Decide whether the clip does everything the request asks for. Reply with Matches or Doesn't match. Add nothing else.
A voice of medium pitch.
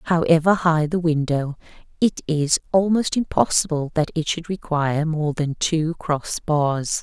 Matches